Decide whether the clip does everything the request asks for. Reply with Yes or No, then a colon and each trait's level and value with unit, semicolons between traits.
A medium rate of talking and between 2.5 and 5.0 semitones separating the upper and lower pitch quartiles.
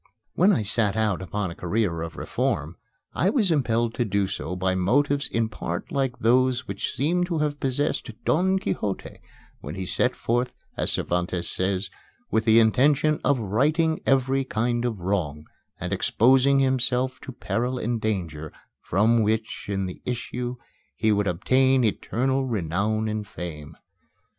No: average, 155 wpm; wide, 5.4 semitones